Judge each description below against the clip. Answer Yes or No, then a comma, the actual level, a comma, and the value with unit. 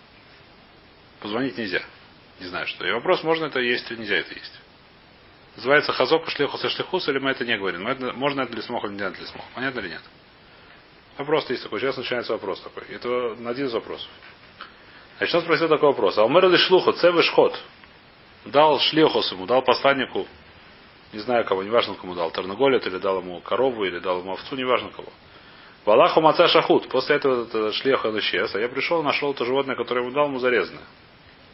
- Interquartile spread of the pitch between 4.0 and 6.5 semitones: Yes, average, 5.2 semitones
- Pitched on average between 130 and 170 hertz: Yes, low, 135 Hz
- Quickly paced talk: Yes, fast, 190 wpm